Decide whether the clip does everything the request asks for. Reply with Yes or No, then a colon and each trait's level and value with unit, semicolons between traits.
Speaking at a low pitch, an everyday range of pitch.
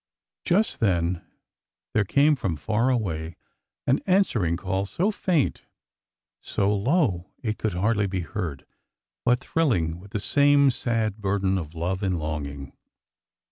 No: low, 100 Hz; wide, 6.2 semitones